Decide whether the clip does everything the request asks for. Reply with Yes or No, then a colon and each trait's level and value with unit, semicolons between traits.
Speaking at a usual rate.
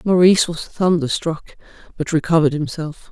No: slow, 115 wpm